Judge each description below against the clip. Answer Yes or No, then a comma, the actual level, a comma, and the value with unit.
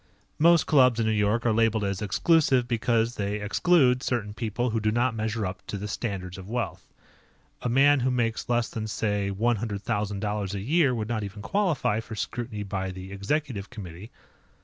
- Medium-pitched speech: No, low, 110 Hz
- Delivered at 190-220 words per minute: Yes, average, 195 wpm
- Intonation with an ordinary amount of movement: Yes, average, 3.2 semitones